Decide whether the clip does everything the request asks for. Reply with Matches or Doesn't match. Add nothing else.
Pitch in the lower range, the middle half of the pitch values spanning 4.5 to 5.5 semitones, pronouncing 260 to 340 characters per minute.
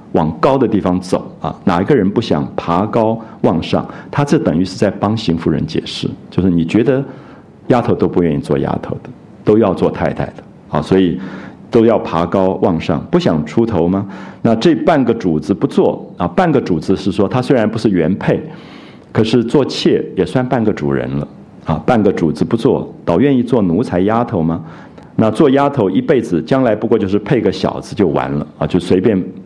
Matches